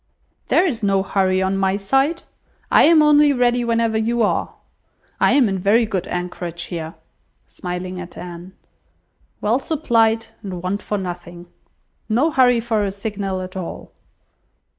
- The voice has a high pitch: Yes, high, 200 Hz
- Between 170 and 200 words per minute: No, average, 150 wpm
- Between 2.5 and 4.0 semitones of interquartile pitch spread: No, average, 4.5 semitones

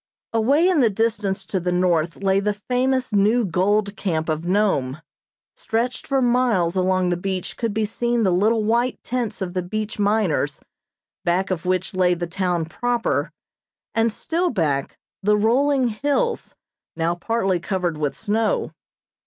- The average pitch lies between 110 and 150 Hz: No, high, 205 Hz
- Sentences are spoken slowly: No, average, 155 wpm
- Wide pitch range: No, average, 4.5 semitones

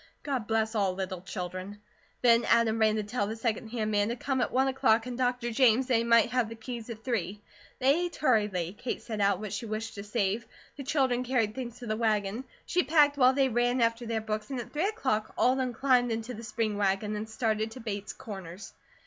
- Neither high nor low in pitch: No, high, 225 Hz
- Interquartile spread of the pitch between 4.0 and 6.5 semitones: No, average, 2.9 semitones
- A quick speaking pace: Yes, fast, 230 wpm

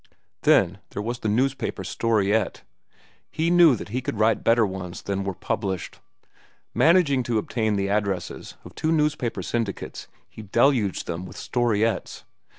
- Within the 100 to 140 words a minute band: No, average, 150 wpm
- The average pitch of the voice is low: Yes, low, 110 Hz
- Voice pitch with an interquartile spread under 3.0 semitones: No, average, 4.3 semitones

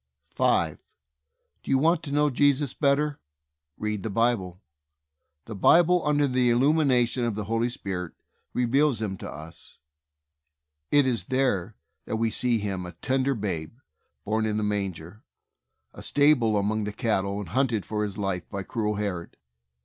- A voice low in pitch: Yes, low, 110 Hz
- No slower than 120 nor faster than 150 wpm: No, average, 160 wpm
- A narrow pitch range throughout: No, average, 5.0 semitones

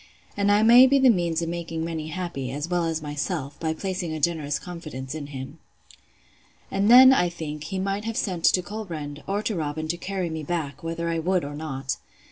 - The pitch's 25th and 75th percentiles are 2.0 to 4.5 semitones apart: Yes, average, 3.8 semitones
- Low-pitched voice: No, medium, 165 Hz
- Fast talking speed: Yes, fast, 210 wpm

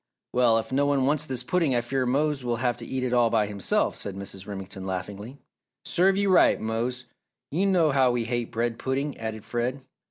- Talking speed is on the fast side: Yes, fast, 210 wpm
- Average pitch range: Yes, average, 3.5 semitones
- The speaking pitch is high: No, low, 125 Hz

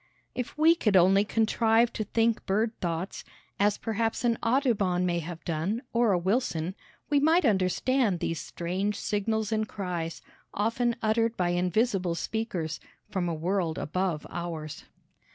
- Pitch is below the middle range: No, high, 200 Hz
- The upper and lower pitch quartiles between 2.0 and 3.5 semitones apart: No, average, 4.5 semitones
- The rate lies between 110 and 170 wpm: Yes, average, 145 wpm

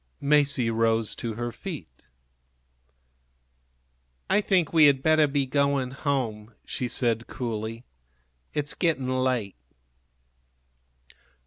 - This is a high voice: No, low, 130 Hz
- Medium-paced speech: No, slow, 100 wpm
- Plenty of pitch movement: No, average, 4.0 semitones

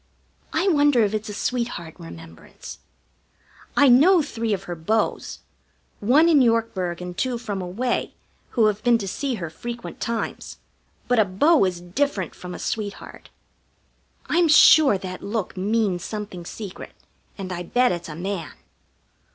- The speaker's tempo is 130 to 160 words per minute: Yes, average, 150 wpm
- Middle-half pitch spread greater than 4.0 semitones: Yes, average, 5.2 semitones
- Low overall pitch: No, high, 215 Hz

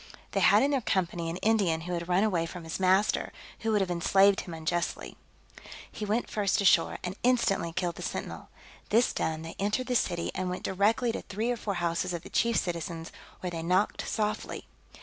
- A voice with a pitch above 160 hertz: Yes, medium, 185 Hz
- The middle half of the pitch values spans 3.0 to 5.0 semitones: Yes, average, 3.8 semitones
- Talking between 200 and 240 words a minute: Yes, fast, 205 wpm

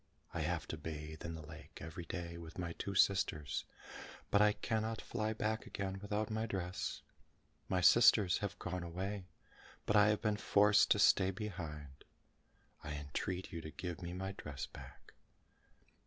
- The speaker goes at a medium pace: Yes, average, 165 wpm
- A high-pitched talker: No, very low, 95 Hz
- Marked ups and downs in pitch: No, average, 3.9 semitones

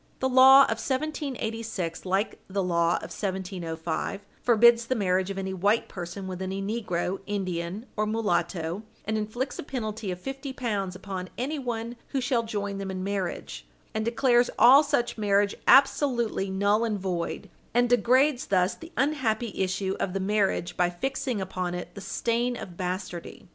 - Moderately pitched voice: No, high, 205 Hz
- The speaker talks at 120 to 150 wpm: No, average, 160 wpm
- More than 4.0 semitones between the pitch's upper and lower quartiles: Yes, average, 4.4 semitones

